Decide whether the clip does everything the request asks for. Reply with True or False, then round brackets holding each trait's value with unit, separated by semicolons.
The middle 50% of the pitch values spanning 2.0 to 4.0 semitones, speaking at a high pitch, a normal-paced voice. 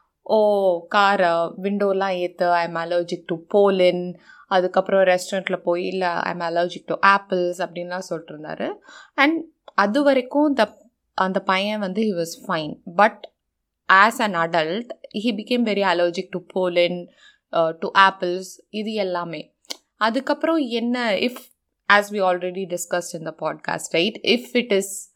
False (3.6 semitones; 195 Hz; 135 wpm)